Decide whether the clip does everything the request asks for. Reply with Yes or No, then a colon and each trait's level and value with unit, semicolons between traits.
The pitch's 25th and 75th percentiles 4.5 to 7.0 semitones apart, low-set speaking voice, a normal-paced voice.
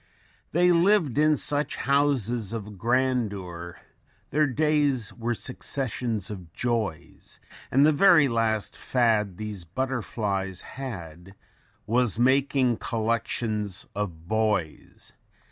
No: average, 4.8 semitones; low, 115 Hz; slow, 100 wpm